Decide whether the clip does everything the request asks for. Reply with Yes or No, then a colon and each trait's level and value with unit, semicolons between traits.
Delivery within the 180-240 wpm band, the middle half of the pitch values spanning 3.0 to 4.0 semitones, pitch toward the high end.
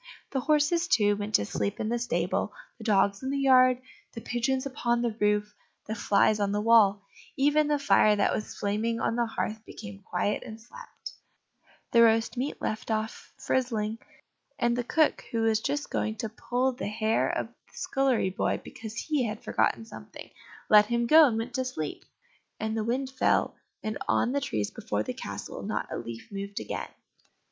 Yes: average, 190 wpm; average, 3.4 semitones; high, 225 Hz